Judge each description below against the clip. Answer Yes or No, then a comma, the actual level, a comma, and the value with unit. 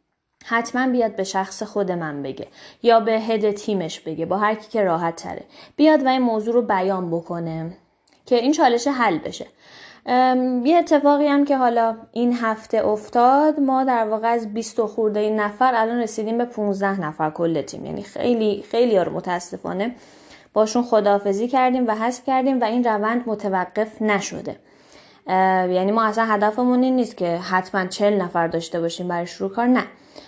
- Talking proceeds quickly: Yes, fast, 170 wpm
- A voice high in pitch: Yes, high, 220 Hz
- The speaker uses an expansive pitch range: No, average, 4.2 semitones